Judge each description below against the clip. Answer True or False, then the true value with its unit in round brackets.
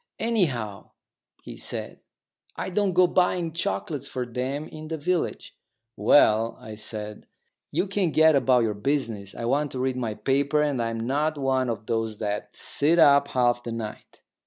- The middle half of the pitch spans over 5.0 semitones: True (5.4 semitones)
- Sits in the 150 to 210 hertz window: False (130 Hz)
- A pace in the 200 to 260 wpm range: False (165 wpm)